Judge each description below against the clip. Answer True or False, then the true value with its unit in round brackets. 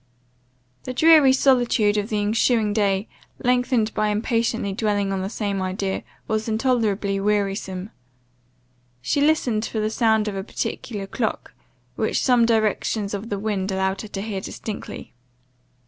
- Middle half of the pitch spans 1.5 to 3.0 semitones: True (2.6 semitones)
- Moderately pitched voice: False (215 Hz)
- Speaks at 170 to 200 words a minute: False (145 wpm)